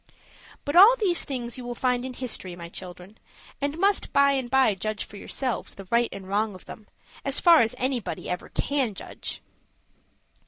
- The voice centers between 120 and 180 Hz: No, high, 245 Hz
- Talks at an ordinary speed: Yes, average, 185 wpm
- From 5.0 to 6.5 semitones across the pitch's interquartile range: Yes, average, 5.3 semitones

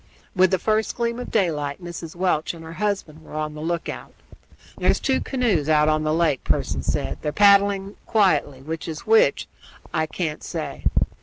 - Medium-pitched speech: Yes, medium, 170 Hz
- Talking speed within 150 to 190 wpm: Yes, average, 175 wpm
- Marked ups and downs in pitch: No, average, 4.7 semitones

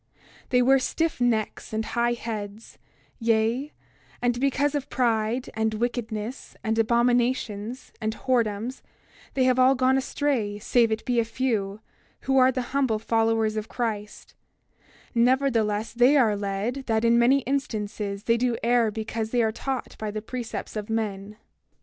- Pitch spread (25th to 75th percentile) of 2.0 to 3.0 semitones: Yes, average, 2.7 semitones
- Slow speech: No, average, 155 wpm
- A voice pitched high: Yes, high, 230 Hz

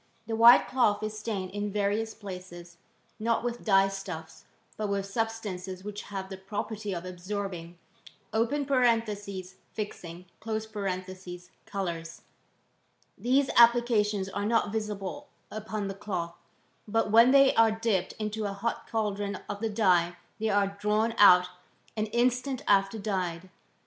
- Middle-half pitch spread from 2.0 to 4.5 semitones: Yes, average, 2.8 semitones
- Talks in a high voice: Yes, high, 205 Hz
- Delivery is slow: Yes, slow, 130 wpm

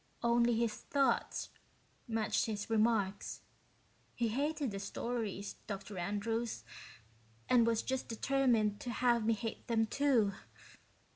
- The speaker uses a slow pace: Yes, slow, 120 wpm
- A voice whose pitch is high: Yes, high, 230 Hz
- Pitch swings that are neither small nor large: No, narrow, 2.2 semitones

